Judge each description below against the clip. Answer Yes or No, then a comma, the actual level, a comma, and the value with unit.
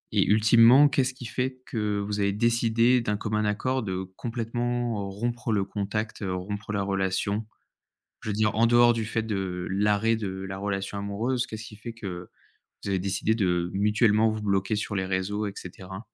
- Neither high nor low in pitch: No, low, 105 Hz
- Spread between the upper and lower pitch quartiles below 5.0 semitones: Yes, average, 2.8 semitones